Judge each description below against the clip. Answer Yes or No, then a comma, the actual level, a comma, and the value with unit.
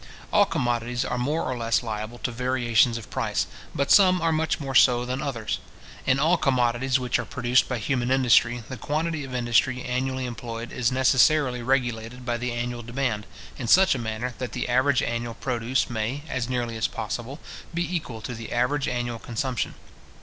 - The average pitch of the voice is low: Yes, low, 125 Hz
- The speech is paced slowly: No, average, 185 wpm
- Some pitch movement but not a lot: No, narrow, 2.0 semitones